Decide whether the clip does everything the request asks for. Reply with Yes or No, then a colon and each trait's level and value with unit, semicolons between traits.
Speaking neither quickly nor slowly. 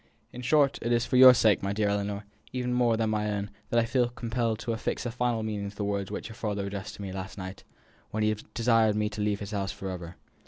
No: fast, 265 wpm